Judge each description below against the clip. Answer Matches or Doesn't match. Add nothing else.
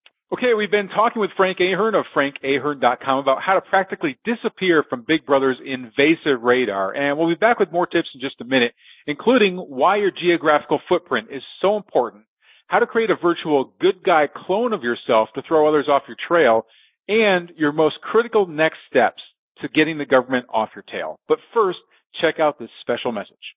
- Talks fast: Doesn't match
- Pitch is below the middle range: Doesn't match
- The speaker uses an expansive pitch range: Matches